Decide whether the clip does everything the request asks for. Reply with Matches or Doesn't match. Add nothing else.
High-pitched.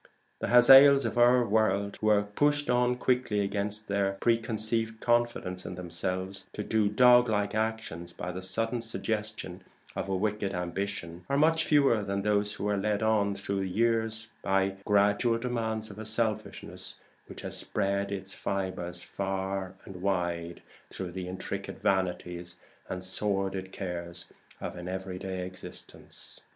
Doesn't match